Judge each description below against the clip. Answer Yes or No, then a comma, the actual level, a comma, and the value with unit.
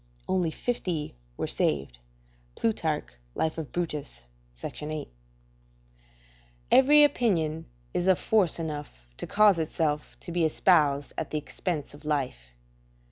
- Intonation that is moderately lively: Yes, average, 3.6 semitones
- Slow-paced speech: Yes, slow, 125 wpm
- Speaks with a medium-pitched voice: Yes, medium, 160 Hz